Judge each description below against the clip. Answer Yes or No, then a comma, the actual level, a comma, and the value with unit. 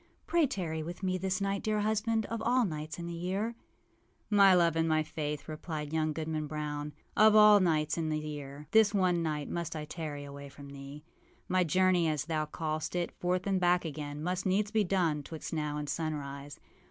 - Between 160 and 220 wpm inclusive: Yes, average, 200 wpm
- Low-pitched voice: No, medium, 165 Hz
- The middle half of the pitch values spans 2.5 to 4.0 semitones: Yes, average, 3.7 semitones